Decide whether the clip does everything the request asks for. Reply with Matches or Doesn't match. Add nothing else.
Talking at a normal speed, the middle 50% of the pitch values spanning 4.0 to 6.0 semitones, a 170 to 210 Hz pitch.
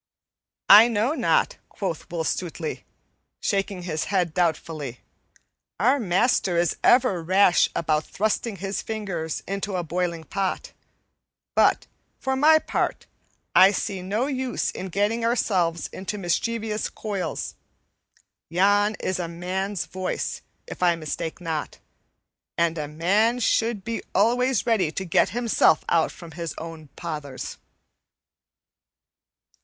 Doesn't match